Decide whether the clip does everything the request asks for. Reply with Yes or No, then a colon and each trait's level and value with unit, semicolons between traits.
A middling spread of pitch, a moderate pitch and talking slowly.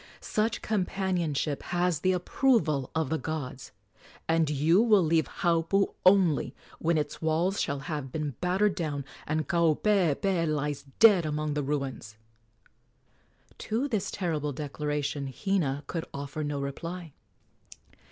Yes: average, 4.0 semitones; medium, 160 Hz; slow, 125 wpm